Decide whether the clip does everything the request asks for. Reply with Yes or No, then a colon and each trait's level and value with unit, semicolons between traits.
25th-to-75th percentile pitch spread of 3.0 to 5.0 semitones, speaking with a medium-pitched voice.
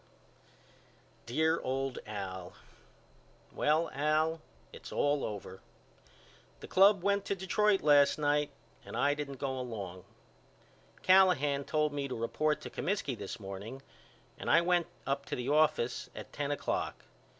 Yes: average, 4.1 semitones; medium, 145 Hz